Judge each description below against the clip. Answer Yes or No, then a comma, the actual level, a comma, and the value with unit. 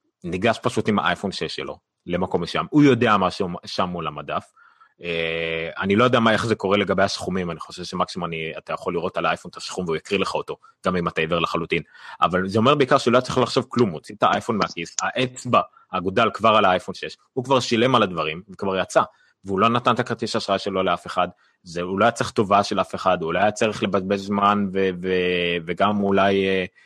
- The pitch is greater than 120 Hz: No, low, 100 Hz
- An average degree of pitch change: Yes, average, 4.4 semitones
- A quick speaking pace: Yes, fast, 220 wpm